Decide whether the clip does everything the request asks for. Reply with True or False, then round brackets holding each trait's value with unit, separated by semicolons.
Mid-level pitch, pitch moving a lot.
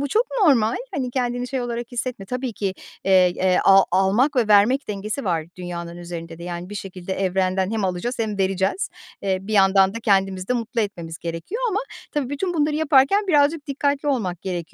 False (210 Hz; 5.9 semitones)